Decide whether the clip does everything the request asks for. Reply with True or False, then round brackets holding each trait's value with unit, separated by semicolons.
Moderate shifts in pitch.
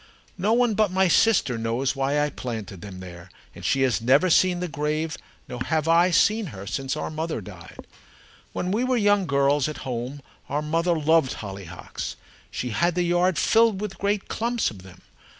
False (7.0 semitones)